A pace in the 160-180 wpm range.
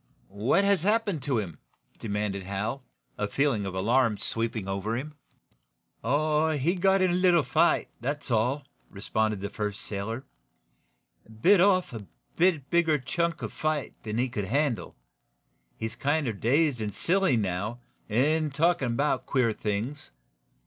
No: average, 150 wpm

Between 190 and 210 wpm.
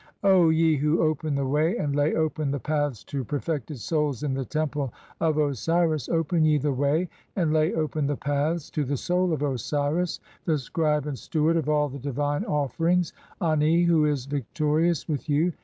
Yes: fast, 205 wpm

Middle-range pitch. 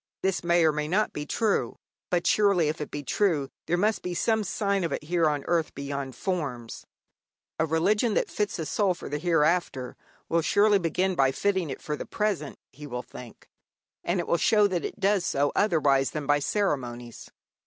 Yes: medium, 165 Hz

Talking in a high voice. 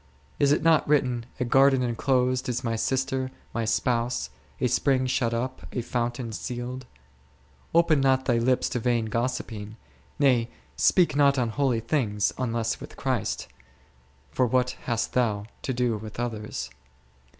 No: low, 125 Hz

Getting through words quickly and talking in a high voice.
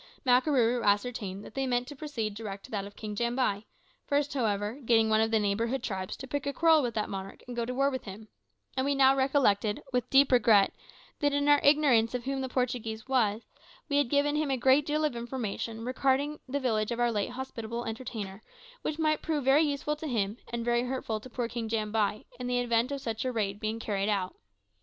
Yes: fast, 220 wpm; high, 240 Hz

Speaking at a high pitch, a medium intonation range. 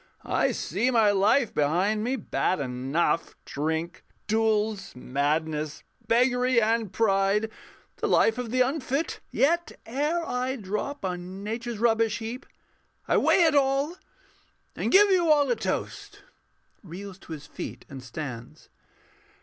No: high, 220 Hz; wide, 6.4 semitones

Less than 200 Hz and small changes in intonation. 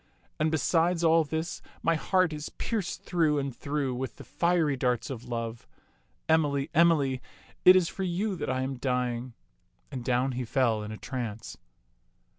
No: medium, 140 Hz; average, 4.8 semitones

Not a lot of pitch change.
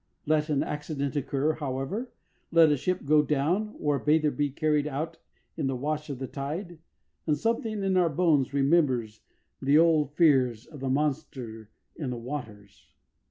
No: average, 3.0 semitones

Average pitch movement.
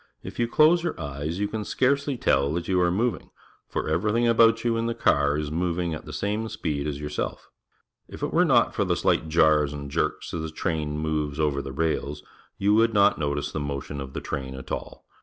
No: wide, 6.7 semitones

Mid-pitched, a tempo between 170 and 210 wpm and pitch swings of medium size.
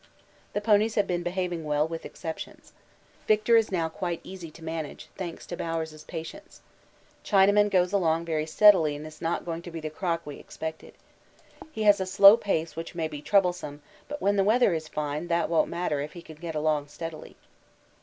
Yes: medium, 170 Hz; average, 195 wpm; average, 3.5 semitones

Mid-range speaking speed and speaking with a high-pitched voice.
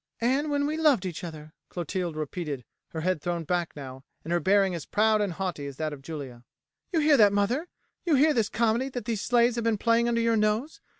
No: fast, 225 wpm; high, 205 Hz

